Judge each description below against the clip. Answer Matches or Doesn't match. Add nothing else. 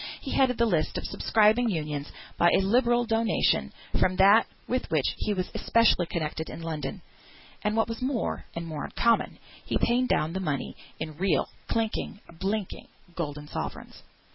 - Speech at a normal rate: Matches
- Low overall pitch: Doesn't match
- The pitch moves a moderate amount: Doesn't match